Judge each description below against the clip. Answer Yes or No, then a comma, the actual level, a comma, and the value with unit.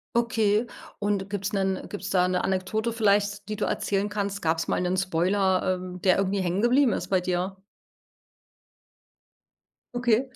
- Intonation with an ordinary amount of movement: No, narrow, 2.1 semitones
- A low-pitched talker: No, high, 195 Hz